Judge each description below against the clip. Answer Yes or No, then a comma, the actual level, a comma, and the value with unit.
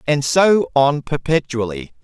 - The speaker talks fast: No, slow, 120 wpm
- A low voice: No, medium, 145 Hz